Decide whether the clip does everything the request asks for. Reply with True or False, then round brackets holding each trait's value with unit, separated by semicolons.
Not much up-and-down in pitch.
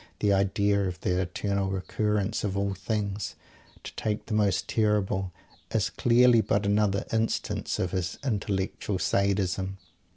True (1.6 semitones)